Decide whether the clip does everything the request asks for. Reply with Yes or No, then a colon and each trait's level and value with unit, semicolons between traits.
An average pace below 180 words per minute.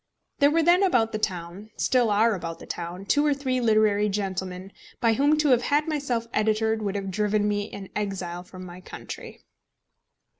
No: average, 185 wpm